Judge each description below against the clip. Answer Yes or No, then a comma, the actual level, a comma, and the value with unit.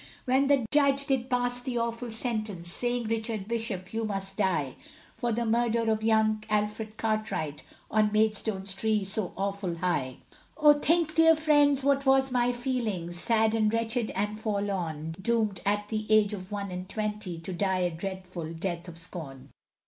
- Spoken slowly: No, average, 165 wpm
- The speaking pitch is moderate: No, high, 215 Hz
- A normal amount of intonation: Yes, average, 3.9 semitones